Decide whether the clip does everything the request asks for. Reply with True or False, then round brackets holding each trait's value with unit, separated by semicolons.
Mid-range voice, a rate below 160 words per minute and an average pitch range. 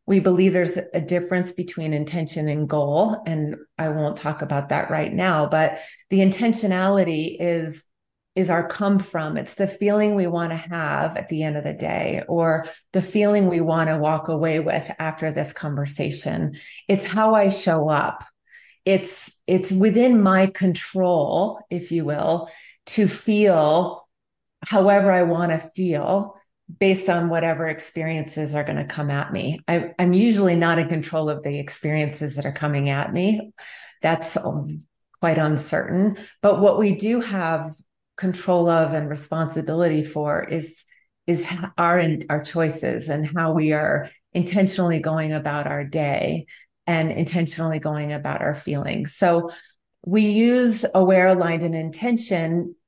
True (170 Hz; 150 wpm; 3.3 semitones)